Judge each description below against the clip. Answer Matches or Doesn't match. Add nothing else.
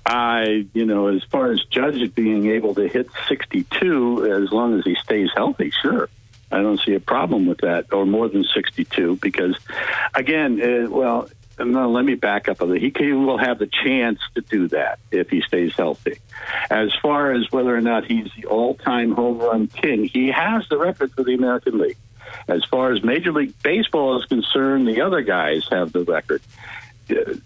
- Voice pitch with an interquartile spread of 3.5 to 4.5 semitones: Doesn't match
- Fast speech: Doesn't match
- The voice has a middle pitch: Doesn't match